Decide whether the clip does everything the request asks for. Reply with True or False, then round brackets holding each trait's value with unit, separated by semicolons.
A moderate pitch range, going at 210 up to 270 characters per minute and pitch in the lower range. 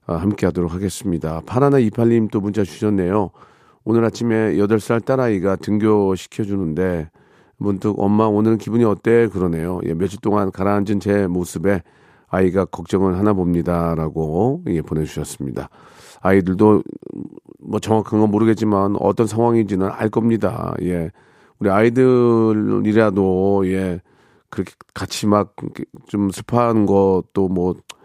False (3.0 semitones; 295 characters per minute; 100 Hz)